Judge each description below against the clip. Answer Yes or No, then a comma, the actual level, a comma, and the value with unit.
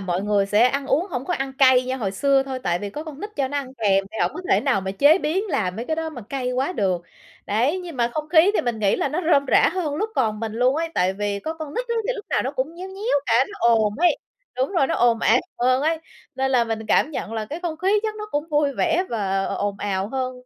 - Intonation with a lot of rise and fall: Yes, wide, 6.4 semitones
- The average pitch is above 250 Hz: Yes, very high, 265 Hz